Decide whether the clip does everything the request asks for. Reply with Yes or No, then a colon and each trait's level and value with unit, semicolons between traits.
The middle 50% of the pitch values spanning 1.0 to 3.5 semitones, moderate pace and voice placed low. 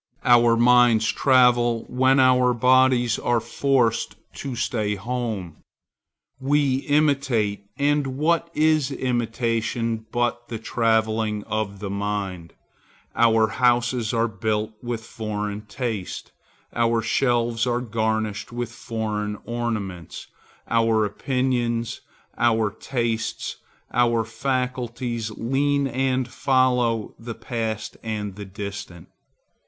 No: narrow, 2.5 semitones; slow, 105 wpm; low, 115 Hz